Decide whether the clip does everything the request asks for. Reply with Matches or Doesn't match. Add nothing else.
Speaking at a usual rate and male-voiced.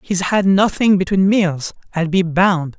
Matches